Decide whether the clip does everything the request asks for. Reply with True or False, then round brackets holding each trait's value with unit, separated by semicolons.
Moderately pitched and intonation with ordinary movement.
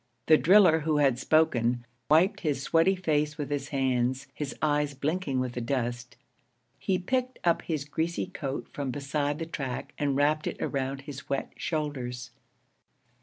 True (145 Hz; 3.0 semitones)